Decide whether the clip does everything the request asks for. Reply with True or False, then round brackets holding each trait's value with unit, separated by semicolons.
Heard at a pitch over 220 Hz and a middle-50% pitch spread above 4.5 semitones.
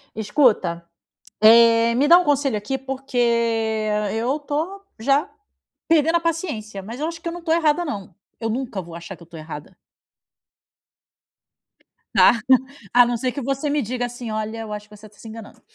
True (245 Hz; 5.4 semitones)